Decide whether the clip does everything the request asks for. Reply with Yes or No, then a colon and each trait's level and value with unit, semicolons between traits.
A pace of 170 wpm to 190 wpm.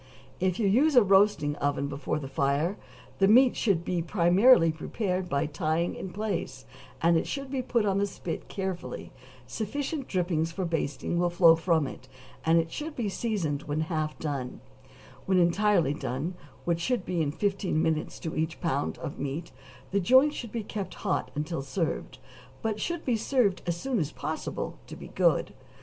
Yes: average, 180 wpm